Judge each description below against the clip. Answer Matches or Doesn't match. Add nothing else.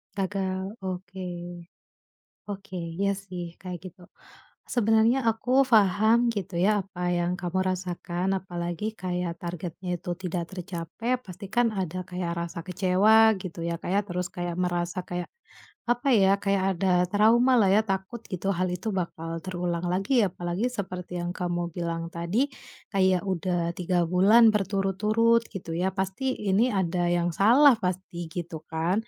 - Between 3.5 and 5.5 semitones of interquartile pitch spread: Doesn't match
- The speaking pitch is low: Doesn't match